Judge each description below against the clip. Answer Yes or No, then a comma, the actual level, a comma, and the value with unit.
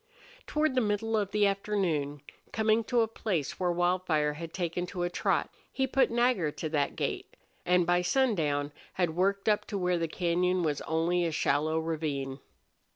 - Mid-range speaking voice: Yes, medium, 180 Hz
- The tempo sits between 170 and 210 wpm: Yes, average, 175 wpm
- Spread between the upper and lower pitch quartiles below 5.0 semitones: Yes, average, 4.4 semitones